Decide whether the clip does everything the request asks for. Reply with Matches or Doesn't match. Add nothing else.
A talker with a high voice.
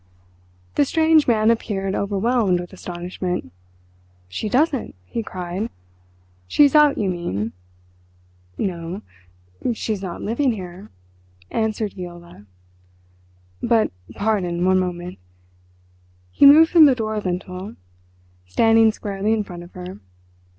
Matches